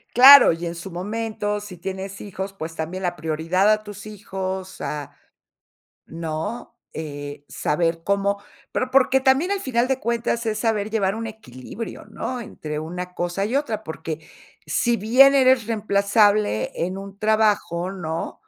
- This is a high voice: Yes, high, 200 Hz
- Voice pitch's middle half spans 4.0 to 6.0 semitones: Yes, average, 4.6 semitones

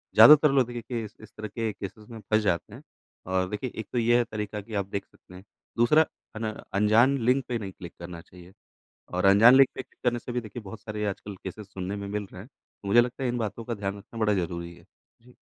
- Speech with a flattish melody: No, average, 3.5 semitones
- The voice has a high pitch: No, low, 110 Hz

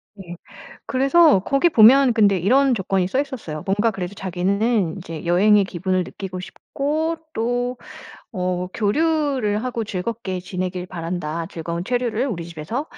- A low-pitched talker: No, high, 200 Hz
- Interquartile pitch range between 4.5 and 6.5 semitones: Yes, wide, 5.4 semitones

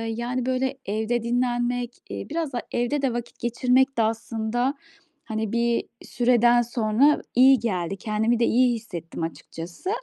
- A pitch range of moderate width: No, narrow, 2.2 semitones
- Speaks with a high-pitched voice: Yes, high, 240 Hz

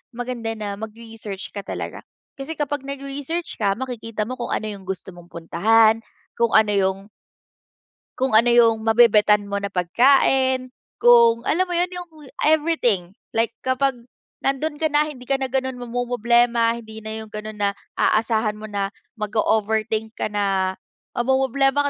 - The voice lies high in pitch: Yes, high, 230 Hz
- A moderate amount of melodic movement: Yes, average, 3.8 semitones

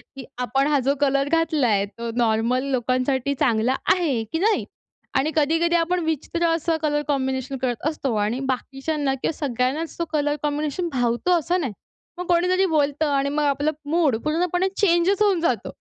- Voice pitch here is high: Yes, very high, 290 Hz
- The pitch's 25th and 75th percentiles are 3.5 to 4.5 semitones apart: Yes, average, 4.1 semitones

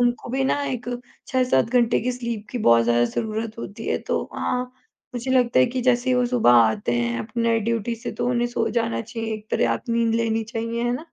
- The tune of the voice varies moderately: No, narrow, 2.0 semitones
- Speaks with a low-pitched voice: No, high, 230 Hz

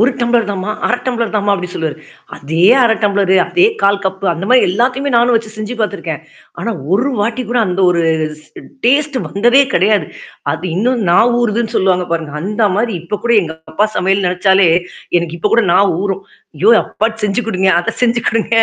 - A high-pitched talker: Yes, high, 205 Hz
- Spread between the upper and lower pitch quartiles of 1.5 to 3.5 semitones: No, average, 4.2 semitones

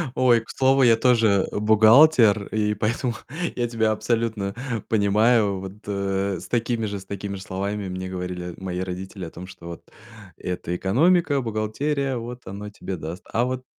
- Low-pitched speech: Yes, low, 105 Hz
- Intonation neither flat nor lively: Yes, average, 3.7 semitones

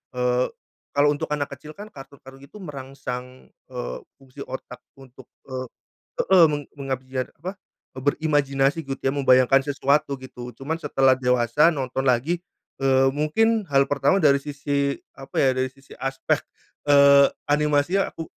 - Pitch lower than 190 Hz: Yes, medium, 140 Hz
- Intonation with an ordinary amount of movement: No, narrow, 2.1 semitones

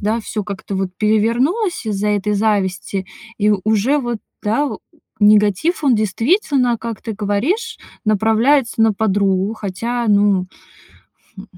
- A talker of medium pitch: No, high, 215 Hz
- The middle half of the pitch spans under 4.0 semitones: Yes, average, 2.9 semitones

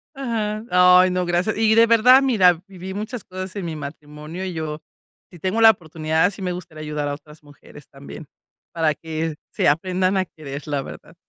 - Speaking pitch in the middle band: Yes, medium, 175 Hz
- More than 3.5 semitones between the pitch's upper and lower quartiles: Yes, average, 4.1 semitones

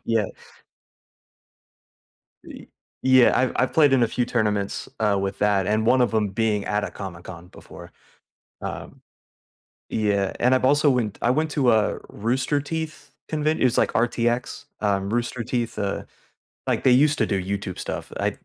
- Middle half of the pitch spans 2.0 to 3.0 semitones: No, average, 4.1 semitones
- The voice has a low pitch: Yes, low, 115 Hz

